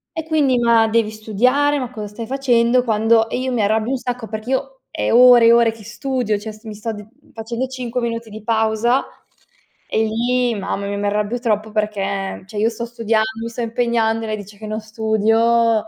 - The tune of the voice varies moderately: No, narrow, 2.1 semitones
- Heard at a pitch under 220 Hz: No, high, 225 Hz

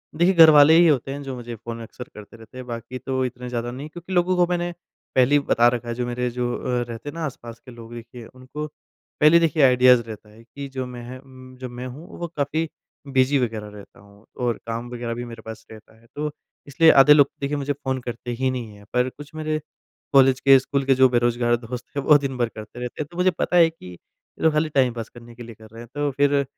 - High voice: No, low, 125 Hz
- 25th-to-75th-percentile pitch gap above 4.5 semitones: No, average, 3.4 semitones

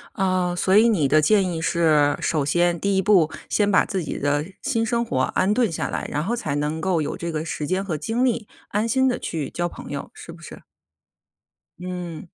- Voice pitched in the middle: Yes, medium, 175 Hz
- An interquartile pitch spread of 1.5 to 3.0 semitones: No, average, 5.0 semitones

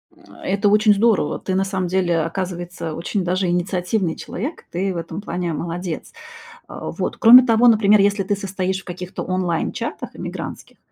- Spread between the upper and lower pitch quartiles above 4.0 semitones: No, narrow, 2.5 semitones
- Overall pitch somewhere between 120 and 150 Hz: No, medium, 185 Hz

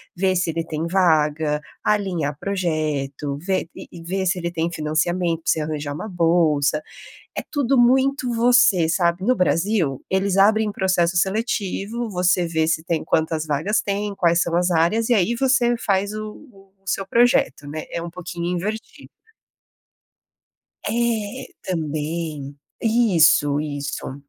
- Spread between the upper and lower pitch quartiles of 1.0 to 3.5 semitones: No, average, 4.6 semitones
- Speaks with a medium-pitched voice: Yes, medium, 175 Hz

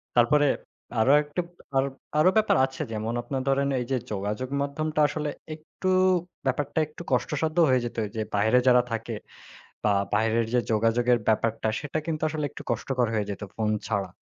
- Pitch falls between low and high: No, low, 125 Hz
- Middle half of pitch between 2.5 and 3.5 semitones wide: No, average, 4.7 semitones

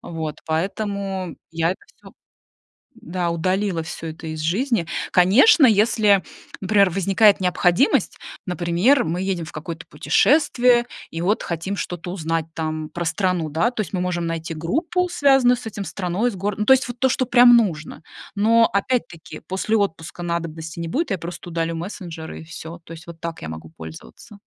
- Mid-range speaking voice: Yes, medium, 180 Hz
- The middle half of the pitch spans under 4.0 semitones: No, average, 4.6 semitones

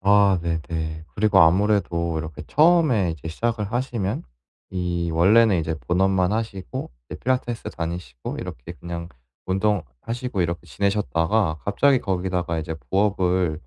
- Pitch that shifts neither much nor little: Yes, average, 4.0 semitones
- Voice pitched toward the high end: No, very low, 95 Hz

